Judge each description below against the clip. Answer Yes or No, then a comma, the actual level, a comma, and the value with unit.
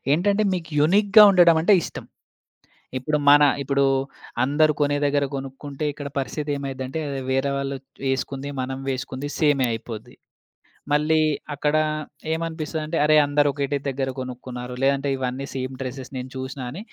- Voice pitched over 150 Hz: No, medium, 140 Hz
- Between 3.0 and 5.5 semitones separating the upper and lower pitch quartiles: No, narrow, 2.5 semitones